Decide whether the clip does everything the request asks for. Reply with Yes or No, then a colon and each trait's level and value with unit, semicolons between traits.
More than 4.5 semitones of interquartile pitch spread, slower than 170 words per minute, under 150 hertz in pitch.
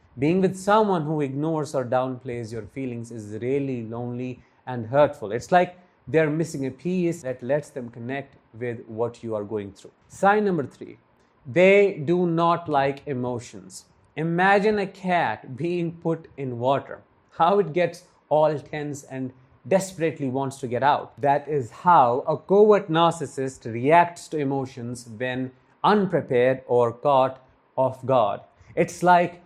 Yes: average, 5.2 semitones; average, 150 wpm; medium, 140 Hz